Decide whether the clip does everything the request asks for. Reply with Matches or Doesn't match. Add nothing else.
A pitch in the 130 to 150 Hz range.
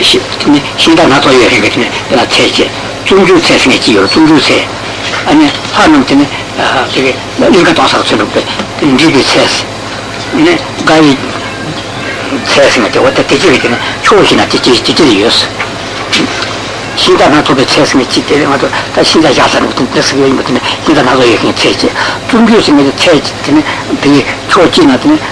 Matches